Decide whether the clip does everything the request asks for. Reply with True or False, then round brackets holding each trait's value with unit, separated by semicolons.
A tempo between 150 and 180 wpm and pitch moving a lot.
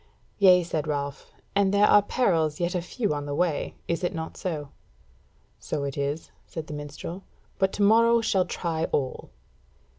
False (175 wpm; 4.7 semitones)